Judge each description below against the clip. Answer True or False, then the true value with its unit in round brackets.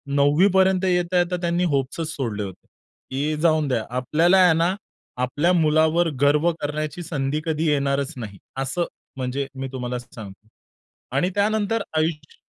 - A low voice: False (155 Hz)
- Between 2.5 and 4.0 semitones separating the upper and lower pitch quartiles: False (4.4 semitones)